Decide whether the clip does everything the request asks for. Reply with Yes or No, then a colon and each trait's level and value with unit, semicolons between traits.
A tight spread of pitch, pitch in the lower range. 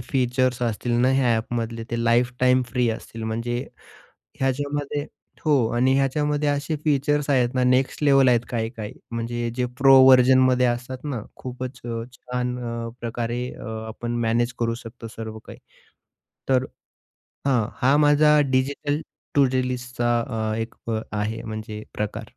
Yes: narrow, 2.2 semitones; low, 125 Hz